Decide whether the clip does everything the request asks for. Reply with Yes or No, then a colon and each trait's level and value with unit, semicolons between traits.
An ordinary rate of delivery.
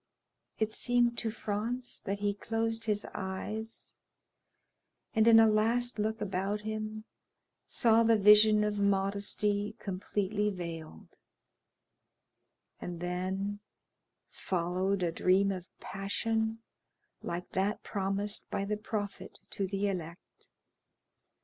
No: slow, 110 wpm